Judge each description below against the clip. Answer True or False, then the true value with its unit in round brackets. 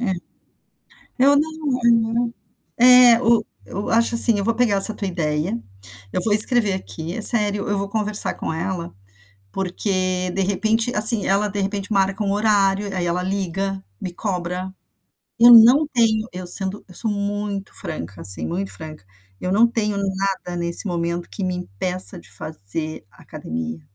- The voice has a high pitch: True (195 Hz)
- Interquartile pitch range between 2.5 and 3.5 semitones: True (3.2 semitones)